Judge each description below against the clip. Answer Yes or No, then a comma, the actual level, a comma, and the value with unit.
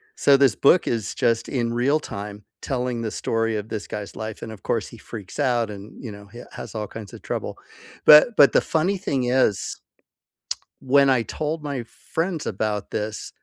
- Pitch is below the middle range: Yes, low, 120 Hz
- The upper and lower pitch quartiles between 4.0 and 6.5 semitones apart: Yes, average, 4.5 semitones